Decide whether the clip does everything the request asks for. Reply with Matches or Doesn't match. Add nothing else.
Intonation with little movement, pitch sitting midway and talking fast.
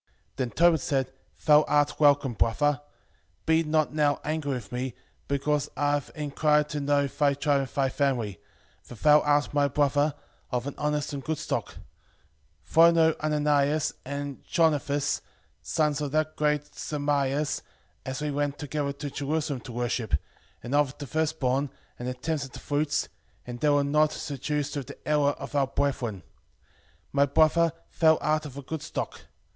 Doesn't match